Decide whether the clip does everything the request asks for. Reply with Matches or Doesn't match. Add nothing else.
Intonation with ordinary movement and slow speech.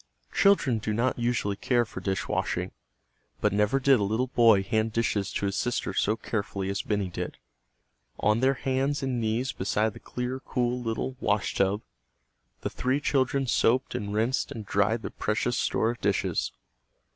Doesn't match